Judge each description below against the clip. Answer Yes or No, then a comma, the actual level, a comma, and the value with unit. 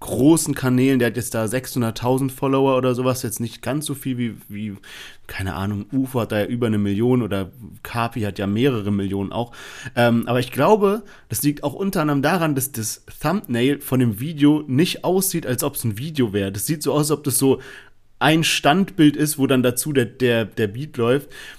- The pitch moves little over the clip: No, average, 4.1 semitones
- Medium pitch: No, low, 125 Hz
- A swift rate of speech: Yes, fast, 210 wpm